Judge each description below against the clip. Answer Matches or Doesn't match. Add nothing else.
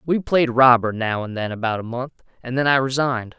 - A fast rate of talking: Matches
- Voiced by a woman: Doesn't match